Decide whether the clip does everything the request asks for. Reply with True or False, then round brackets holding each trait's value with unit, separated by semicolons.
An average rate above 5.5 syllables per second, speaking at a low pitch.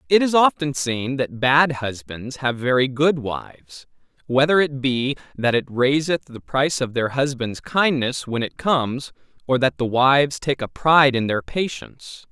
False (4.5 syllables/s; 130 Hz)